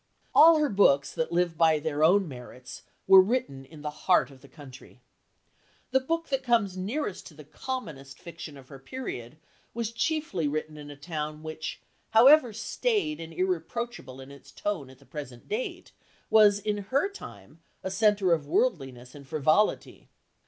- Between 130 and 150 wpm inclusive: No, average, 165 wpm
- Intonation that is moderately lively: No, wide, 7.9 semitones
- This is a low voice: No, medium, 170 Hz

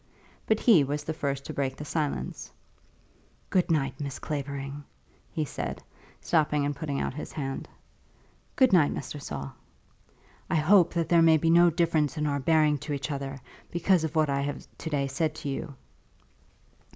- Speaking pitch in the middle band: Yes, medium, 150 Hz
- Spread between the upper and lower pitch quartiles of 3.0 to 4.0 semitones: No, narrow, 2.6 semitones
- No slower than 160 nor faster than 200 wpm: Yes, average, 175 wpm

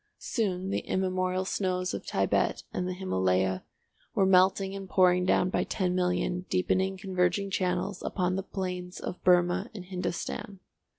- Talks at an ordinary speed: Yes, average, 145 wpm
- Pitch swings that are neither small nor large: No, narrow, 1.0 semitones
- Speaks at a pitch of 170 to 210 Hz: Yes, medium, 185 Hz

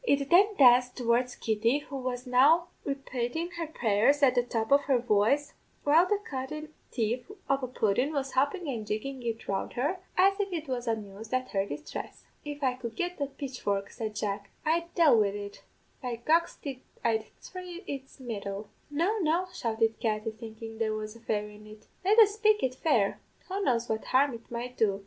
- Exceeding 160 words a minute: Yes, average, 190 wpm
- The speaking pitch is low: No, very high, 255 Hz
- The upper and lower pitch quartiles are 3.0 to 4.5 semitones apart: No, average, 5.2 semitones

